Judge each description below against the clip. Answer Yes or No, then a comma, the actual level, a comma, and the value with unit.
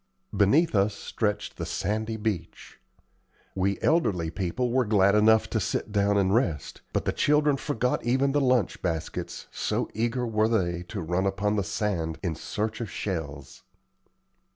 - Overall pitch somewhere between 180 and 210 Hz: No, low, 105 Hz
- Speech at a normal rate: Yes, average, 155 wpm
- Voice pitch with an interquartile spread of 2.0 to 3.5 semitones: No, average, 3.9 semitones